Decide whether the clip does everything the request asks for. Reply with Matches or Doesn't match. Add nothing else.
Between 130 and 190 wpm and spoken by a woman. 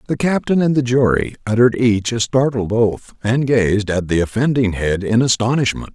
Doesn't match